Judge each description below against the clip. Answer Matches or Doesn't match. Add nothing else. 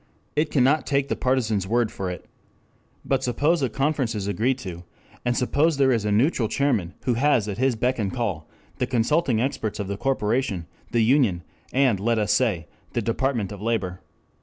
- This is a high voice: Doesn't match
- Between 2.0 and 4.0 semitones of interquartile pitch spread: Doesn't match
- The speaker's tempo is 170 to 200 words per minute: Matches